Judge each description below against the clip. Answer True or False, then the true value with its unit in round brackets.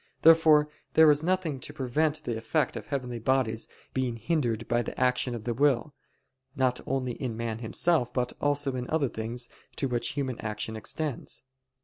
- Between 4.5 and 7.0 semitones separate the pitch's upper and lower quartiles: False (3.7 semitones)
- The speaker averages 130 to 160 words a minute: False (170 wpm)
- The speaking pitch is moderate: False (130 Hz)